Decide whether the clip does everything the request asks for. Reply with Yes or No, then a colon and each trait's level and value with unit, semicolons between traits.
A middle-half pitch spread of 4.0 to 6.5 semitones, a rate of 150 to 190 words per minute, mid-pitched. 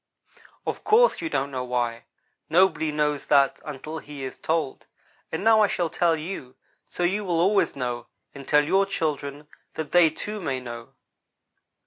Yes: average, 4.5 semitones; average, 165 wpm; medium, 155 Hz